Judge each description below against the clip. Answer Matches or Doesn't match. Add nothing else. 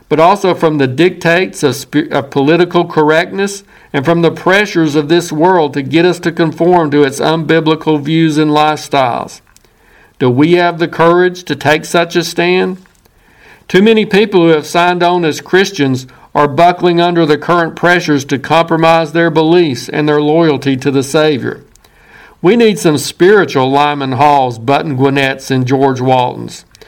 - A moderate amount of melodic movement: Matches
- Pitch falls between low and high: Matches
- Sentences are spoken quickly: Doesn't match